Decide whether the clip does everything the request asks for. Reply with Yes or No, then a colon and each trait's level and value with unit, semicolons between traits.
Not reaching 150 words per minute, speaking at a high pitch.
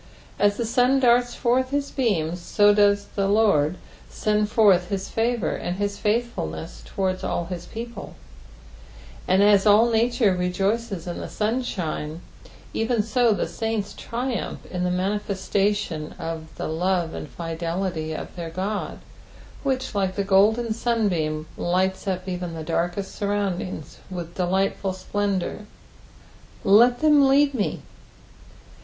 Yes: slow, 135 wpm; high, 200 Hz